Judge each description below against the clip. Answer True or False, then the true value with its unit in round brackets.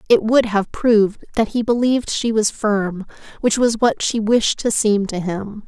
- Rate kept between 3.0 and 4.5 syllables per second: True (4.4 syllables/s)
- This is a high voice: True (220 Hz)